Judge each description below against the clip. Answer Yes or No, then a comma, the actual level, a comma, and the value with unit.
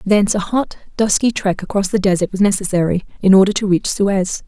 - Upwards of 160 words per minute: Yes, average, 200 wpm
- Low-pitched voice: No, high, 195 Hz